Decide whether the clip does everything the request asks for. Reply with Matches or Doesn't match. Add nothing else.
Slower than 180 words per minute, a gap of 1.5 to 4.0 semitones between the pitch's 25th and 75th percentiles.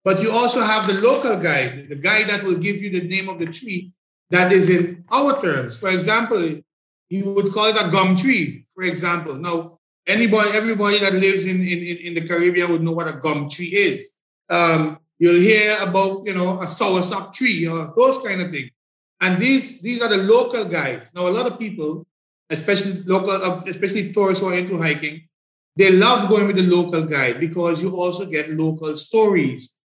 Doesn't match